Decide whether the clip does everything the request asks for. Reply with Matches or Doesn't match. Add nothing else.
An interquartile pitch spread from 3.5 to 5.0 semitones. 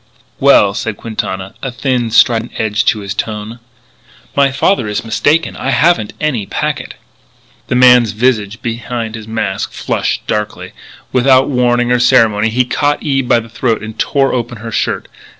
Doesn't match